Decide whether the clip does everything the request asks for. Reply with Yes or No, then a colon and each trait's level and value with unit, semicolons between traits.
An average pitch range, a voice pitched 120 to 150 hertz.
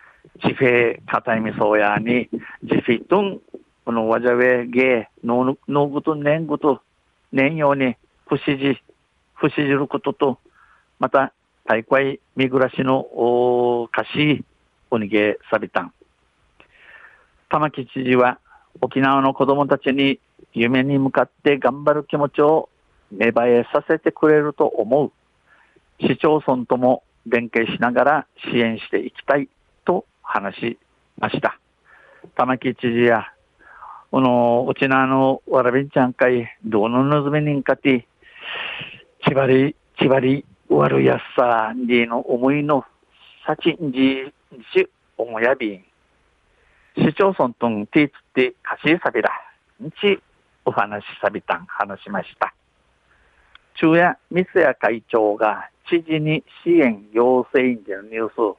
Yes: average, 3.4 semitones; low, 130 Hz